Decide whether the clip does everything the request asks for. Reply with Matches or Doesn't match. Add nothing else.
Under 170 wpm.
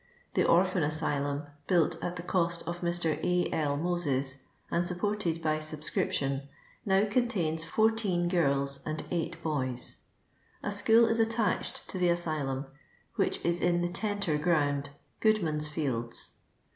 Matches